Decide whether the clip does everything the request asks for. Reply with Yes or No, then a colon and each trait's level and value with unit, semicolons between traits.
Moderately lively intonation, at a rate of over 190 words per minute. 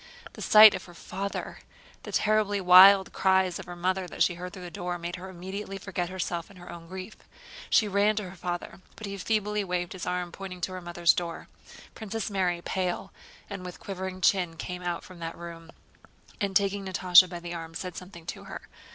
No: narrow, 2.0 semitones; fast, 205 wpm